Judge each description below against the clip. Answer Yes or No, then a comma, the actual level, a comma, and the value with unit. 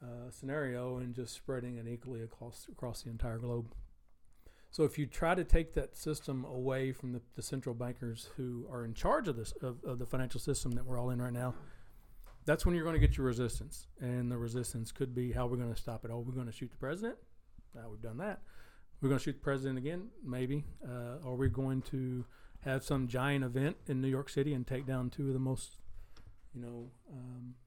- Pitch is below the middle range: Yes, low, 125 Hz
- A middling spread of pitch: No, narrow, 1.9 semitones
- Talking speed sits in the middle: No, fast, 230 wpm